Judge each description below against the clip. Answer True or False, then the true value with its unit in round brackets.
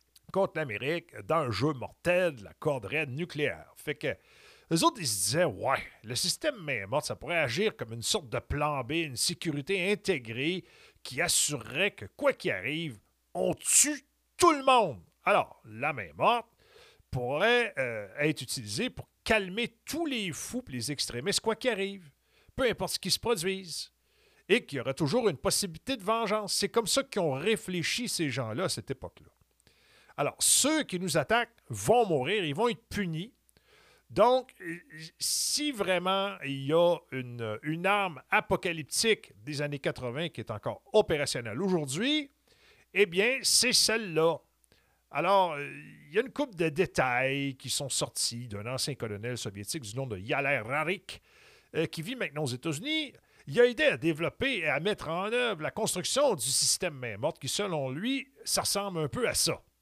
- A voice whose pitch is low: False (170 Hz)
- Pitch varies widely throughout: True (7.5 semitones)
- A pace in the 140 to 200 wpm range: True (170 wpm)